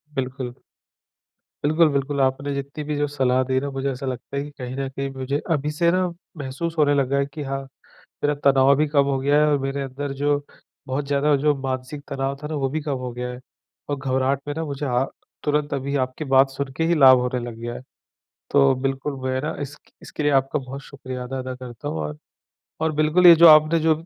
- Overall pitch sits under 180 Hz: Yes, medium, 140 Hz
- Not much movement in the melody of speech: Yes, narrow, 1.9 semitones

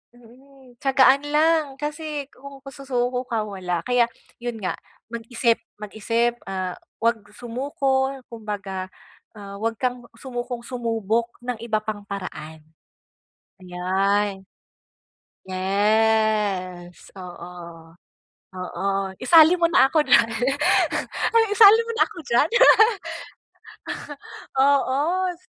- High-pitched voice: Yes, high, 230 Hz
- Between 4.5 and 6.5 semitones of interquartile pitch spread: Yes, average, 5.2 semitones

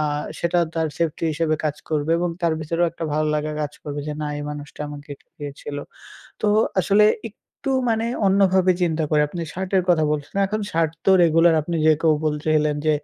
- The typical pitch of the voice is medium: Yes, medium, 160 Hz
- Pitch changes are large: No, average, 2.7 semitones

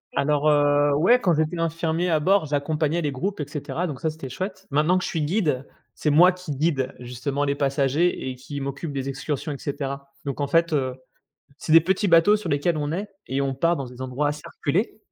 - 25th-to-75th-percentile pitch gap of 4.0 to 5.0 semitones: No, average, 3.3 semitones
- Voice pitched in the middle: Yes, medium, 150 Hz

